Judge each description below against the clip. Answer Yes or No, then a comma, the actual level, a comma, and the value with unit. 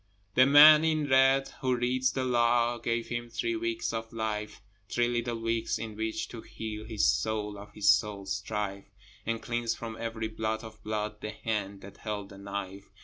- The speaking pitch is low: Yes, low, 115 Hz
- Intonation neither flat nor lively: No, narrow, 2.1 semitones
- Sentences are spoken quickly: No, average, 185 wpm